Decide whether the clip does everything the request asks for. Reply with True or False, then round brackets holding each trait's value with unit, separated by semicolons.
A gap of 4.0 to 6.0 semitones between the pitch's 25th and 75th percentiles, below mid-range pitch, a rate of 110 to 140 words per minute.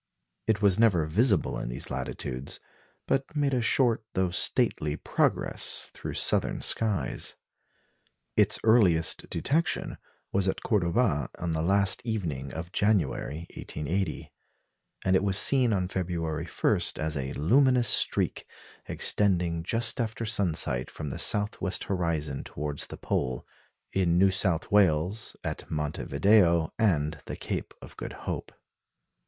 True (5.4 semitones; 95 Hz; 135 wpm)